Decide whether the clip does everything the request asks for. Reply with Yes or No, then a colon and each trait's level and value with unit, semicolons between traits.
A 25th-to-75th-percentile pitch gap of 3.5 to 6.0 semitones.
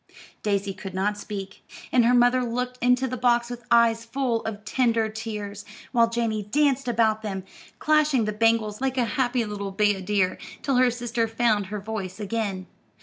No: average, 2.8 semitones